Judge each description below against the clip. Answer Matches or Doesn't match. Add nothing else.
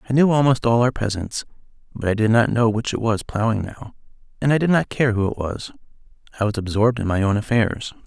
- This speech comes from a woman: Doesn't match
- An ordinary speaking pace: Doesn't match